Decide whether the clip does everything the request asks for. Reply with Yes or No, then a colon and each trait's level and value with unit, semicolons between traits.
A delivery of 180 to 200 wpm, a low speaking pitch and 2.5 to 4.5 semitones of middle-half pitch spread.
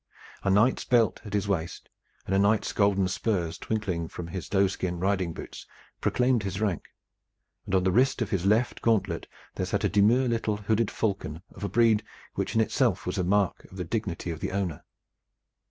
Yes: average, 190 wpm; low, 100 Hz; average, 3.1 semitones